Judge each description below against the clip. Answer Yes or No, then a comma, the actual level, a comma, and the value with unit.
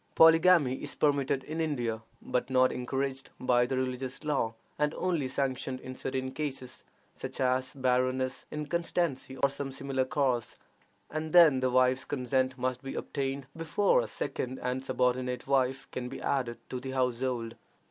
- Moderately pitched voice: No, low, 130 Hz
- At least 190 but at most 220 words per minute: No, average, 155 wpm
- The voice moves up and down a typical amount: No, narrow, 1.7 semitones